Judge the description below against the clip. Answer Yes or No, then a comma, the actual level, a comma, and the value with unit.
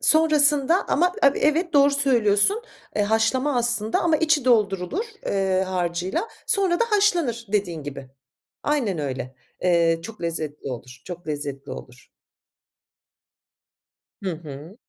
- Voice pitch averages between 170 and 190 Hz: No, high, 215 Hz